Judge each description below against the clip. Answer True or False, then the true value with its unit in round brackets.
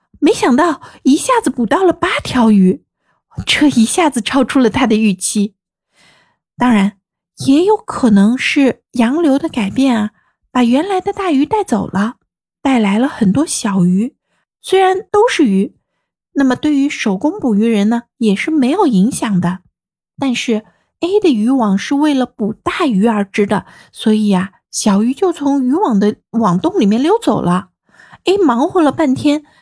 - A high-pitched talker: True (250 Hz)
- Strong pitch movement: True (6.2 semitones)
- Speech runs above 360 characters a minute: False (230 characters per minute)